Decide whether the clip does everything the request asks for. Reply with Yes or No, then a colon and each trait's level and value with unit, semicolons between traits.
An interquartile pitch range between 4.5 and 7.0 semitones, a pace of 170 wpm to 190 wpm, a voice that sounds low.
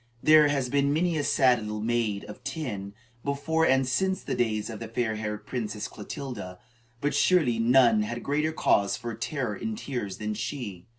Yes: average, 5.1 semitones; average, 180 wpm; low, 120 Hz